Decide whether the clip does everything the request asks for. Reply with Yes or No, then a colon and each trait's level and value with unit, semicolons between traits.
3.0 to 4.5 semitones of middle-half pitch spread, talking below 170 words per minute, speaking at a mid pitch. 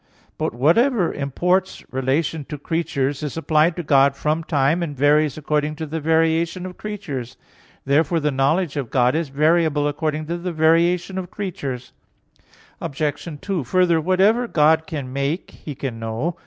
Yes: average, 3.4 semitones; average, 160 wpm; medium, 155 Hz